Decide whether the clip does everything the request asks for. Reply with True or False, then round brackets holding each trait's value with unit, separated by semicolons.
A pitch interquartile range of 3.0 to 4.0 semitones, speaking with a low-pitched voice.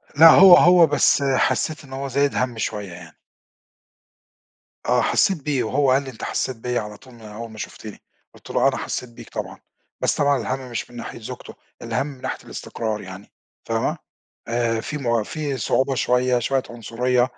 True (3.4 semitones; 125 Hz)